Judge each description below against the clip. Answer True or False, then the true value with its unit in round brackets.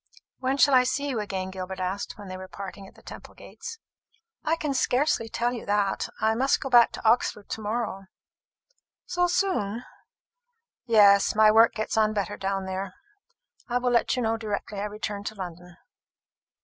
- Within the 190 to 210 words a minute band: False (180 wpm)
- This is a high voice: True (215 Hz)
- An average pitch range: True (3.8 semitones)